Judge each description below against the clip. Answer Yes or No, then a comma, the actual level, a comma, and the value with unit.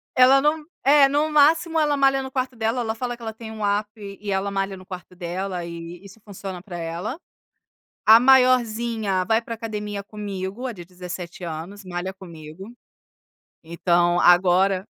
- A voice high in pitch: Yes, high, 205 Hz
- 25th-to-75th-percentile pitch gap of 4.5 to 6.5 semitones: Yes, average, 5.0 semitones